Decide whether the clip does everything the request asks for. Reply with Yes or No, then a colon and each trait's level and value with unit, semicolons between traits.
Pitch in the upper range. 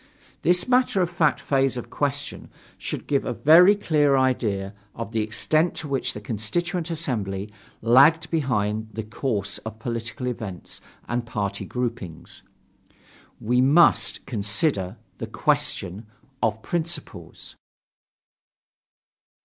No: low, 125 Hz